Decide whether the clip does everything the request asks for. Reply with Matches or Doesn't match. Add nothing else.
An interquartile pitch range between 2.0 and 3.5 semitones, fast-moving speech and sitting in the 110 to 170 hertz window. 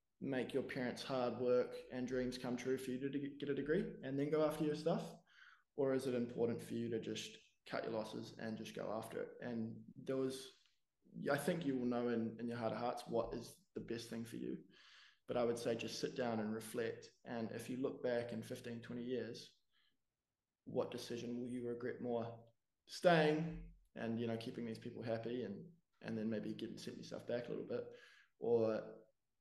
Matches